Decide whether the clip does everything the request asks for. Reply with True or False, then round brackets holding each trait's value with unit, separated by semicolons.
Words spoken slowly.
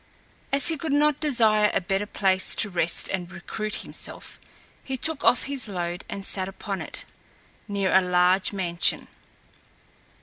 False (155 wpm)